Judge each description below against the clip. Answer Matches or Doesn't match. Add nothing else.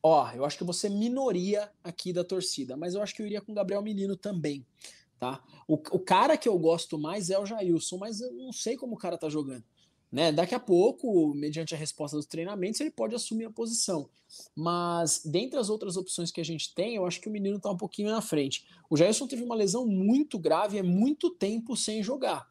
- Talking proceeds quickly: Matches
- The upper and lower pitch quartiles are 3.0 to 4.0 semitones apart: Doesn't match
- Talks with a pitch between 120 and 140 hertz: Doesn't match